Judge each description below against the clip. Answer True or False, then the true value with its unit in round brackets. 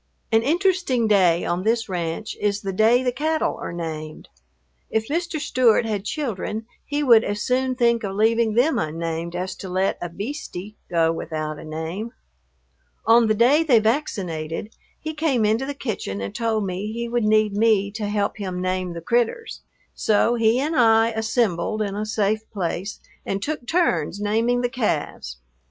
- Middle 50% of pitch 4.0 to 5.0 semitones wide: True (4.5 semitones)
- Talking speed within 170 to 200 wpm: True (175 wpm)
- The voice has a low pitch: False (215 Hz)